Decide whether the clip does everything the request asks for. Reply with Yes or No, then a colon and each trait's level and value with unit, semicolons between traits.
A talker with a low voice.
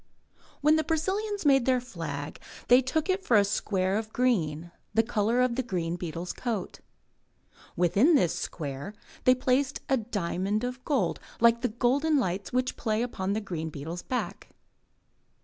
No: high, 225 Hz